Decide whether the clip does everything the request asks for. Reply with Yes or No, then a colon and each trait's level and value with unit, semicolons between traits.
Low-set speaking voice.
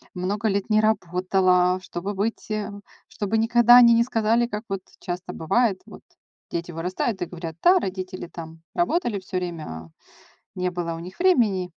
No: high, 190 Hz